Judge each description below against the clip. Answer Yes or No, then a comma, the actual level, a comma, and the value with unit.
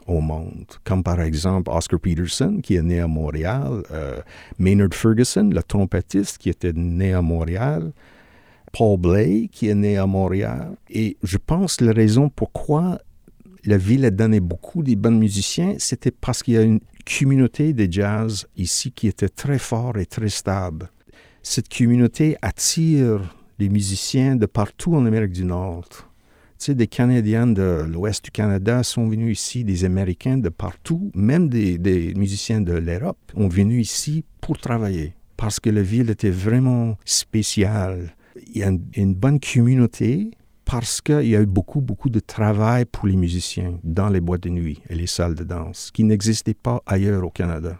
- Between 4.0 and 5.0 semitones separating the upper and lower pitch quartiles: Yes, average, 4.7 semitones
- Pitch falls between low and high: No, low, 105 Hz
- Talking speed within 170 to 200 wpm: Yes, average, 175 wpm